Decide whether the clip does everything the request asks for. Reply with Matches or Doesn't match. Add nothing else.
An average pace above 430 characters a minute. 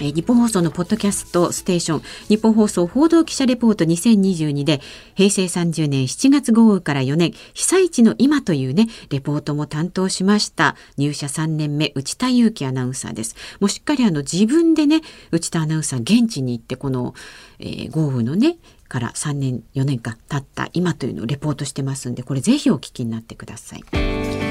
Doesn't match